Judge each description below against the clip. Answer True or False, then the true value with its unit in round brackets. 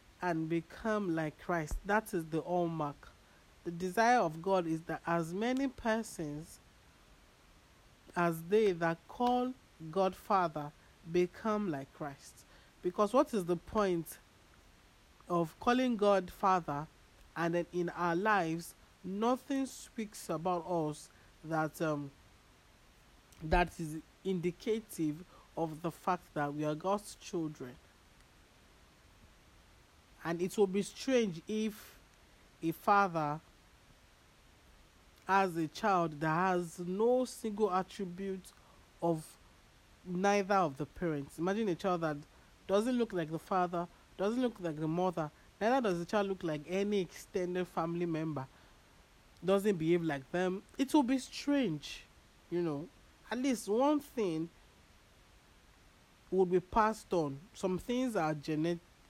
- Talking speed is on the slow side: True (125 wpm)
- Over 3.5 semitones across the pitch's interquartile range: True (4.2 semitones)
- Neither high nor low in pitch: True (175 Hz)